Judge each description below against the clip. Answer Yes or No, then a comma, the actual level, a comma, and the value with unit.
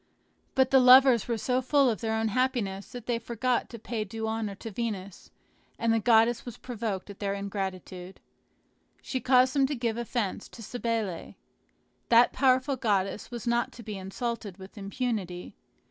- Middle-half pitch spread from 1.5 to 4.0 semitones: Yes, average, 3.6 semitones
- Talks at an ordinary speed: Yes, average, 170 wpm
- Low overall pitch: No, high, 230 Hz